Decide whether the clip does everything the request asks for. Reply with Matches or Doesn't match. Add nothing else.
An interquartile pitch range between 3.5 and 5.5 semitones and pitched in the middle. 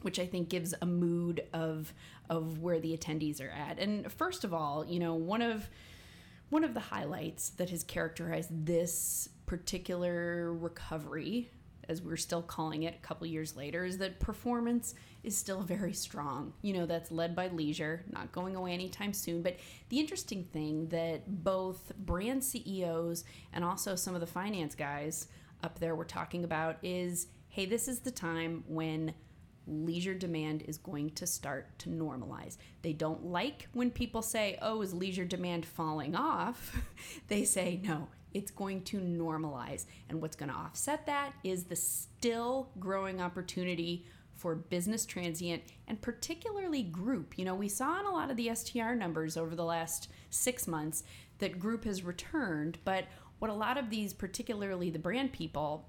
Matches